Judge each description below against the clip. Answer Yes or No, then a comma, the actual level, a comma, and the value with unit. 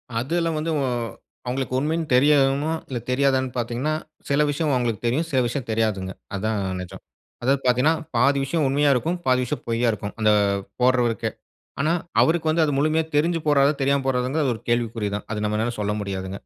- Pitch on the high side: No, low, 130 Hz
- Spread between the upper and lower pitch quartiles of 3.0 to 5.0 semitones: Yes, average, 4.2 semitones